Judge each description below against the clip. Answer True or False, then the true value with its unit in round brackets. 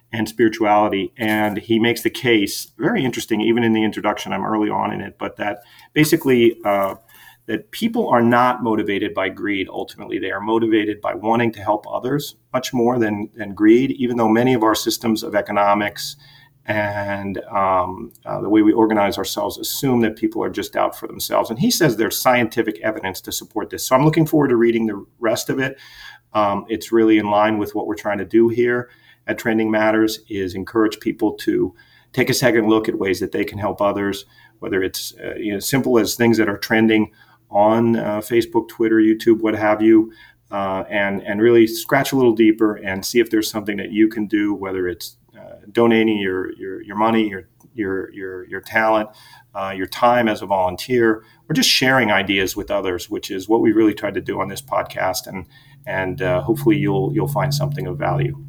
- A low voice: True (110 Hz)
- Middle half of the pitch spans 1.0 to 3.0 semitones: True (2.5 semitones)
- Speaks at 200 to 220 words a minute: True (205 wpm)